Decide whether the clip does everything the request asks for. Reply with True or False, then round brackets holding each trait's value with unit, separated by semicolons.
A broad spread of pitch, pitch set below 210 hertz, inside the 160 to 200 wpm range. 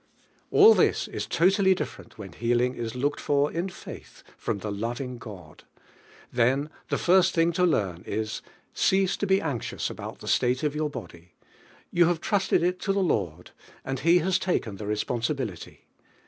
True (8.2 semitones; 140 Hz; 180 wpm)